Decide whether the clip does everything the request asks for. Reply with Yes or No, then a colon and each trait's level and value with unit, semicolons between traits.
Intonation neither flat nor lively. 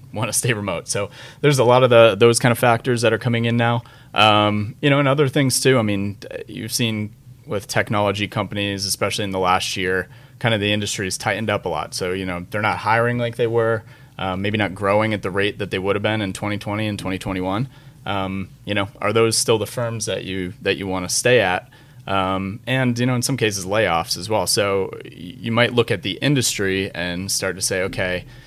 Yes: average, 3.7 semitones